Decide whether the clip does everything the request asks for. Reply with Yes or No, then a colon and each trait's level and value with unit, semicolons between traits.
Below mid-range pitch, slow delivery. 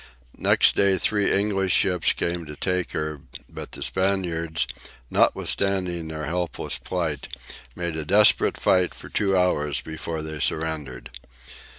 Yes: very low, 85 Hz; slow, 130 wpm